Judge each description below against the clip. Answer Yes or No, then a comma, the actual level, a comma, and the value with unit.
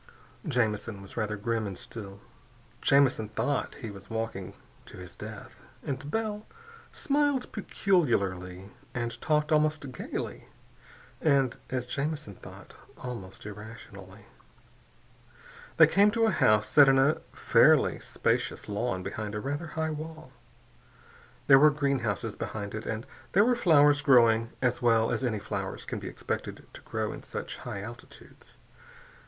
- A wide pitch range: Yes, wide, 6.1 semitones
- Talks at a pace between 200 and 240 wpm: No, average, 140 wpm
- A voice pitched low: Yes, low, 125 Hz